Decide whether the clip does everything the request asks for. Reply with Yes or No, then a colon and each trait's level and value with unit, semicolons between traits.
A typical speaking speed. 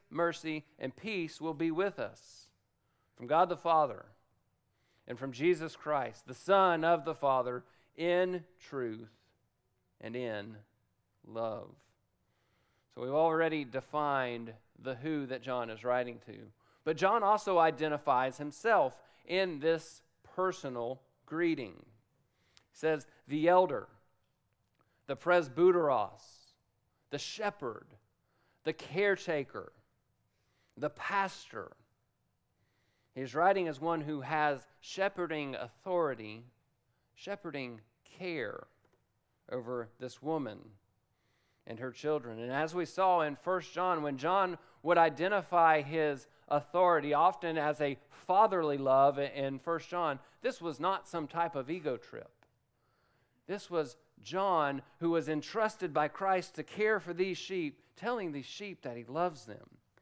No: slow, 120 wpm